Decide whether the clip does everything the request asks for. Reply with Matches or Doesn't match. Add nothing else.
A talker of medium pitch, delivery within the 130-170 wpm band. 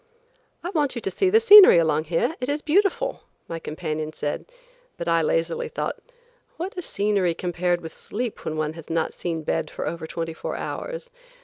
Doesn't match